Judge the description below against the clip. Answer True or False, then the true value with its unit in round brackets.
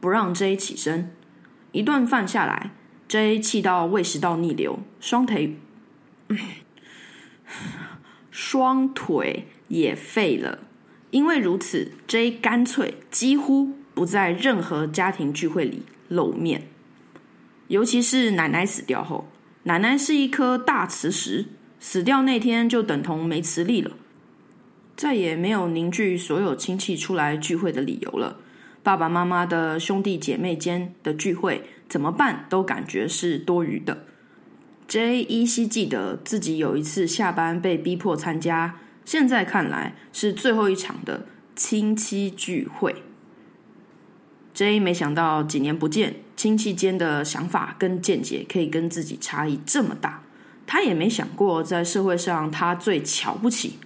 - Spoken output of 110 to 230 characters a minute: True (205 characters per minute)